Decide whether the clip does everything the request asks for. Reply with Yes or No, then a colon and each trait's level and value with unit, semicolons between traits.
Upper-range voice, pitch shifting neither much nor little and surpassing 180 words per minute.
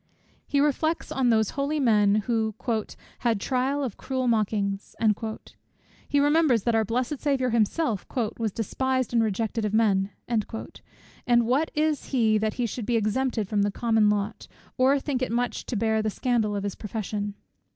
No: high, 230 Hz; average, 3.5 semitones; average, 165 wpm